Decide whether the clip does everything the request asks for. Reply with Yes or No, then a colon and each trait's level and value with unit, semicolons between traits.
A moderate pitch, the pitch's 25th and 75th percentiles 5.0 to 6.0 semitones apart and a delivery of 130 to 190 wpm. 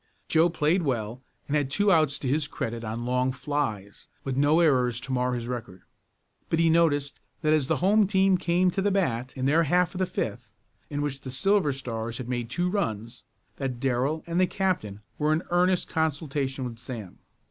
No: medium, 145 Hz; average, 5.3 semitones; average, 200 wpm